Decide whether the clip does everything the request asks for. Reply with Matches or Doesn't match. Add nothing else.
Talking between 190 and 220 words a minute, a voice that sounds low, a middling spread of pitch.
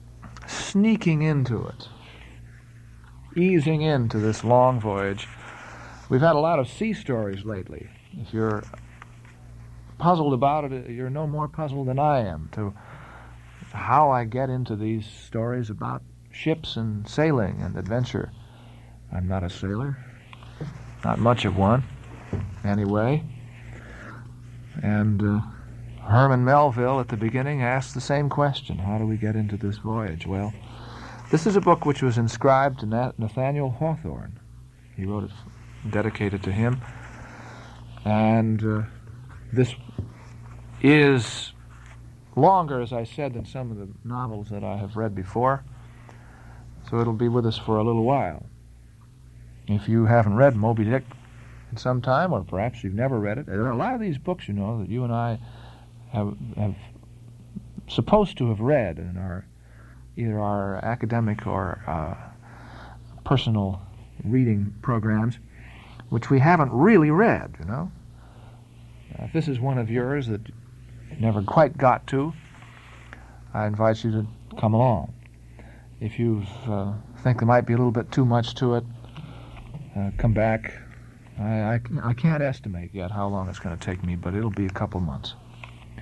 Doesn't match